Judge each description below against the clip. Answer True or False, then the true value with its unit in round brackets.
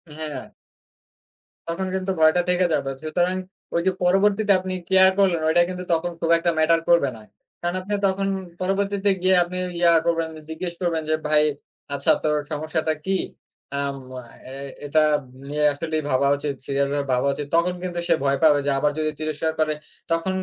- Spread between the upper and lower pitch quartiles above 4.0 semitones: False (3.3 semitones)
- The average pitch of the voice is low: False (165 Hz)